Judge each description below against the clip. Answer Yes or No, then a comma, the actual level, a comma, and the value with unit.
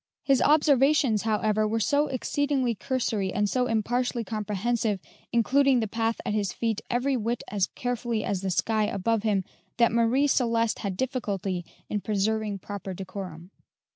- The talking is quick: No, average, 150 wpm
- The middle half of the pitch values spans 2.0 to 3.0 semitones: No, average, 3.4 semitones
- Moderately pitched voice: No, high, 225 Hz